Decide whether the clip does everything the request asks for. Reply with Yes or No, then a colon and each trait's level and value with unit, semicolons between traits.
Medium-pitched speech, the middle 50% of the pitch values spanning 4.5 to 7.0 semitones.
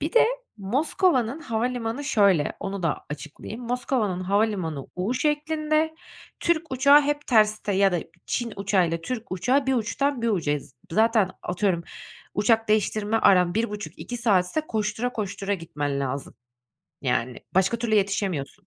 No: high, 215 Hz; average, 5.2 semitones